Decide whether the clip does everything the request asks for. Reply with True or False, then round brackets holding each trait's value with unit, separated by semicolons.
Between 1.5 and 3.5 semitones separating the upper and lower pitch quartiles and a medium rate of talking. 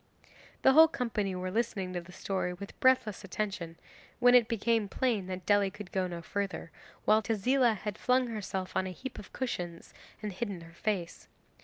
False (4.1 semitones; 180 wpm)